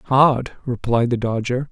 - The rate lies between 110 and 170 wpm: Yes, average, 140 wpm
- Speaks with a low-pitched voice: Yes, low, 125 Hz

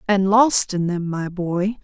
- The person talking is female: Yes, female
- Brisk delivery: No, average, 195 wpm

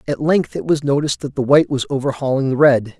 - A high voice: No, medium, 140 Hz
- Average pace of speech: No, fast, 240 wpm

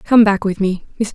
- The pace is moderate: No, fast, 210 wpm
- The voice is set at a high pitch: Yes, high, 205 Hz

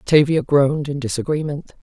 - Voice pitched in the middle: Yes, medium, 145 Hz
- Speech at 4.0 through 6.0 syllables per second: Yes, 5.3 syllables/s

